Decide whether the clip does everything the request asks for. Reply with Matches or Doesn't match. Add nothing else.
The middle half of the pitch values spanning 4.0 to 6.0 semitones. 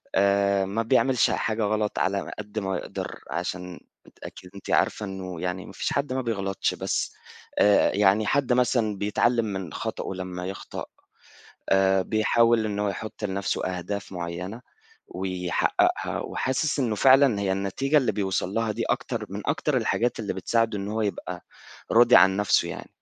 Doesn't match